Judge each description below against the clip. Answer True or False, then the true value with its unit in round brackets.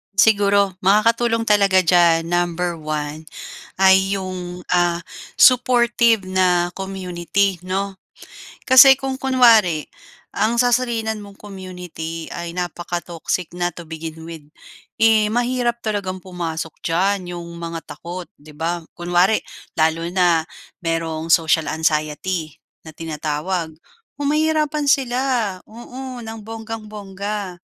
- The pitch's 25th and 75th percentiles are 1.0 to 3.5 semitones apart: False (4.7 semitones)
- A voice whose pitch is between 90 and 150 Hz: False (185 Hz)